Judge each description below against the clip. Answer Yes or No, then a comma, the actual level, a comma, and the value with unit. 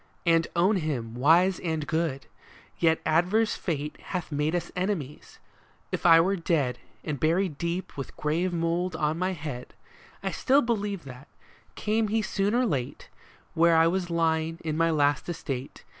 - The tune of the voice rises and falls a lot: No, average, 3.4 semitones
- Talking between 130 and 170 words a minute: Yes, average, 160 wpm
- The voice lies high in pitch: No, medium, 165 Hz